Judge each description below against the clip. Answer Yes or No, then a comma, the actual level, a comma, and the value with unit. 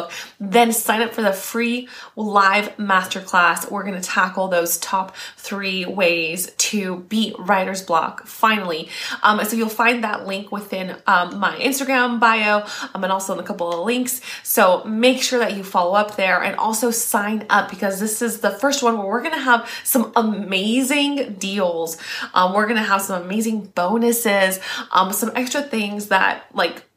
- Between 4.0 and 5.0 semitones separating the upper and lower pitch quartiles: No, average, 3.6 semitones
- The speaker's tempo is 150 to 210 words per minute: Yes, average, 170 wpm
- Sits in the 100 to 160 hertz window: No, high, 205 Hz